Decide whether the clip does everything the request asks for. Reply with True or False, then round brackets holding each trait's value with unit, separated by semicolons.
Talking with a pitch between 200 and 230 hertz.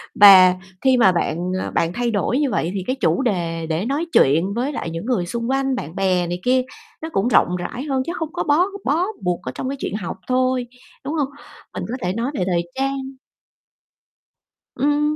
False (240 Hz)